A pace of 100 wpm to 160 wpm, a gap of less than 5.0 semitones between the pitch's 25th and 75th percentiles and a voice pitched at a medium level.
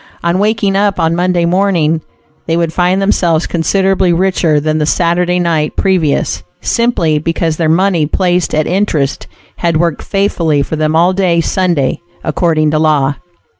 Yes: average, 155 wpm; average, 3.0 semitones; medium, 170 Hz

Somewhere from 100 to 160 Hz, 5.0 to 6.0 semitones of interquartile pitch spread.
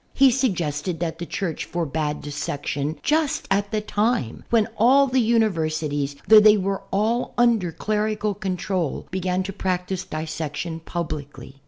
No: medium, 185 Hz; average, 5.3 semitones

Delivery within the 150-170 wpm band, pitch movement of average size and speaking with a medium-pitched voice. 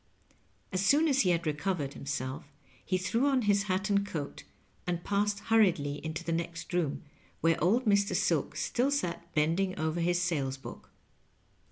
Yes: average, 165 wpm; average, 4.1 semitones; medium, 180 Hz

